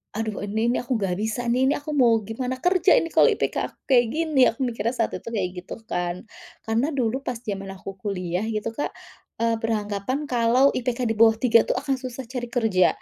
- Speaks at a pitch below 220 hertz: No, high, 230 Hz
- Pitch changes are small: No, average, 3.3 semitones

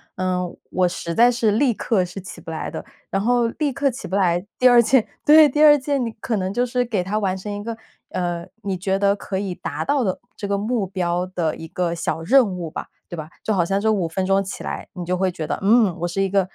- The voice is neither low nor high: No, high, 195 Hz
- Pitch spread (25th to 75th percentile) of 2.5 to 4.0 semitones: No, average, 4.4 semitones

